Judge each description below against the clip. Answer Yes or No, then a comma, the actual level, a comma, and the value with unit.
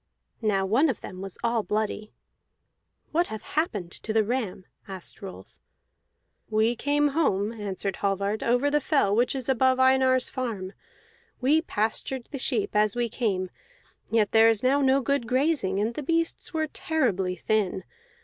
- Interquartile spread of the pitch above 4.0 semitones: Yes, average, 4.7 semitones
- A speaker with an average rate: Yes, average, 160 wpm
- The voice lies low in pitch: No, high, 230 Hz